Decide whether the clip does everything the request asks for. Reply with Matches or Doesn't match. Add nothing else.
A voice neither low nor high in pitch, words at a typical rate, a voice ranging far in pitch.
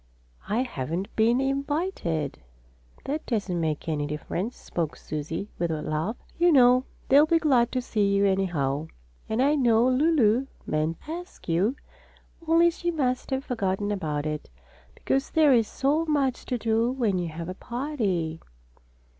Doesn't match